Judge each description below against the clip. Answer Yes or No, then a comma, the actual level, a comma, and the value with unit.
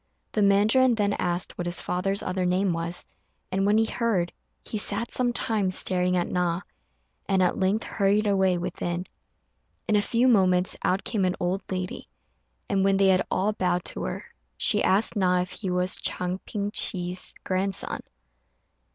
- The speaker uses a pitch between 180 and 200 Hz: Yes, high, 190 Hz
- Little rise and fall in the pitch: Yes, narrow, 2.1 semitones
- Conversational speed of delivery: Yes, average, 170 wpm